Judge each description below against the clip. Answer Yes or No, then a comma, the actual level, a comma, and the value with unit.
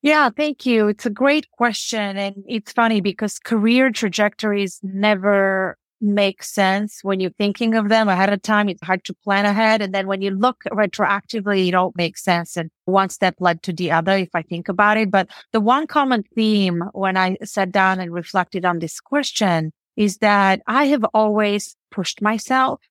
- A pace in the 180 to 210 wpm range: Yes, average, 190 wpm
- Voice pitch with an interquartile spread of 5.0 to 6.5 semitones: No, narrow, 2.5 semitones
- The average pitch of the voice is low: No, high, 205 Hz